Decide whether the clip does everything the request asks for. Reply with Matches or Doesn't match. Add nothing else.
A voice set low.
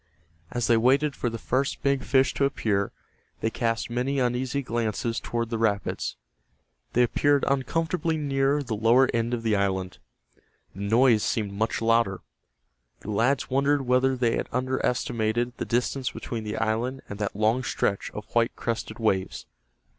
Matches